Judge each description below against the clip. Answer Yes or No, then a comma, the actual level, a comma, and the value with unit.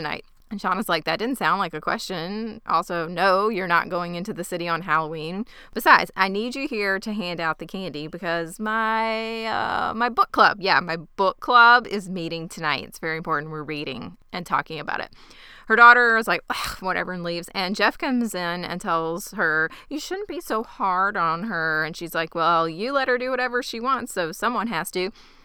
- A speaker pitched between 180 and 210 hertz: Yes, medium, 185 Hz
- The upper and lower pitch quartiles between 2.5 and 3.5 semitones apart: No, average, 5.3 semitones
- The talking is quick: Yes, fast, 210 wpm